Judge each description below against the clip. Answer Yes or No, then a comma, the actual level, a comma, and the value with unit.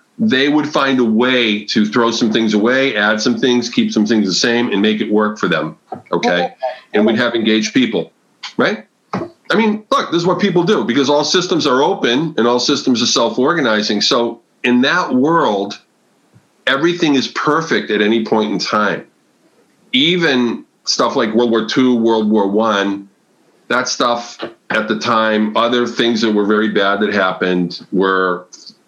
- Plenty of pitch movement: No, average, 3.1 semitones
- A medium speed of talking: Yes, average, 175 wpm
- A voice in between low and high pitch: No, low, 115 Hz